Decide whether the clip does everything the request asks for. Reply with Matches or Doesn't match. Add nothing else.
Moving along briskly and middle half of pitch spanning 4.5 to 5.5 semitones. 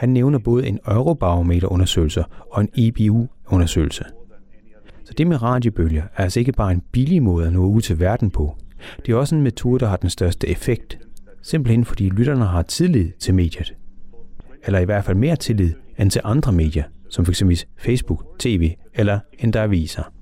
Doesn't match